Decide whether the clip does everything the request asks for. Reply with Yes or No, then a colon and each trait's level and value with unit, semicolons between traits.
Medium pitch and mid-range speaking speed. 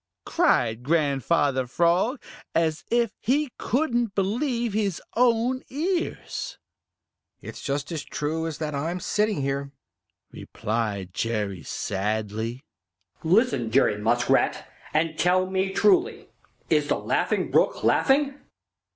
No: medium, 170 Hz; slow, 110 wpm